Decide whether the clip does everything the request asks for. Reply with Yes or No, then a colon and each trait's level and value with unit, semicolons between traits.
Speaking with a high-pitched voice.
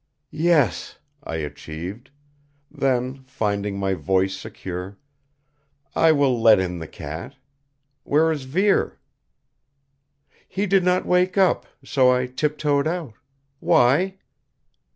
No: low, 130 Hz